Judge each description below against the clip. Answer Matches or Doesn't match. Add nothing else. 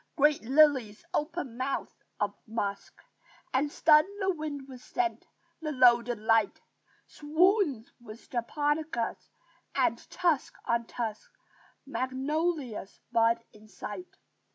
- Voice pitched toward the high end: Matches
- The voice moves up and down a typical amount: Matches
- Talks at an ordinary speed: Doesn't match